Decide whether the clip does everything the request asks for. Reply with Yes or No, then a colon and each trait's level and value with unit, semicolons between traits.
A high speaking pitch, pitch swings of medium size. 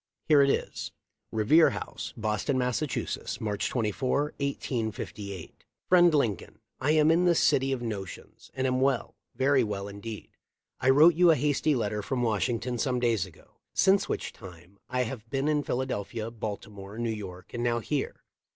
No: low, 120 Hz; average, 4.6 semitones